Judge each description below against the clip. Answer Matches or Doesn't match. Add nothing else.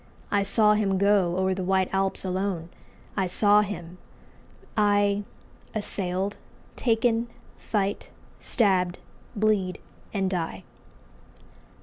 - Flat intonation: Matches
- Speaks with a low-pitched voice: Doesn't match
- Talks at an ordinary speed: Doesn't match